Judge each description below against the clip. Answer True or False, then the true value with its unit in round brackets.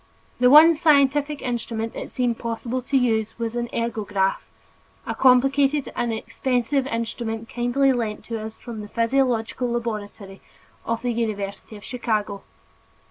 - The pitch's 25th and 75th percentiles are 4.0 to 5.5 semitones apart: False (2.6 semitones)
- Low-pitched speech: False (235 Hz)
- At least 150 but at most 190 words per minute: False (135 wpm)